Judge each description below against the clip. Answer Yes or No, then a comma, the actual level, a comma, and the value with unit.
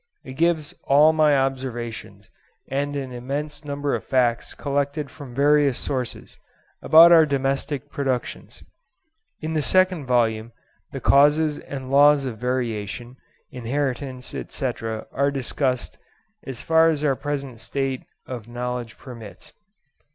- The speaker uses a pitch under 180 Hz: Yes, low, 135 Hz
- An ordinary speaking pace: No, slow, 125 wpm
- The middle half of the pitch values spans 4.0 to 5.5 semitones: No, average, 2.8 semitones